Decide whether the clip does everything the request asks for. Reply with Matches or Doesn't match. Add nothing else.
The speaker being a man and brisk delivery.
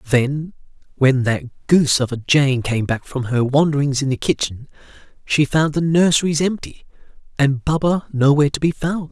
Doesn't match